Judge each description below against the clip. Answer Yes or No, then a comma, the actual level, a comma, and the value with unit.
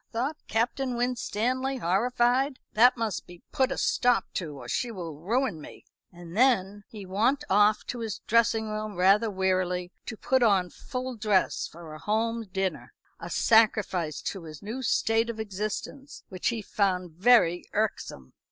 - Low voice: No, high, 215 Hz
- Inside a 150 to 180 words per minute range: Yes, average, 160 wpm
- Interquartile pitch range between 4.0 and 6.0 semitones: Yes, average, 4.5 semitones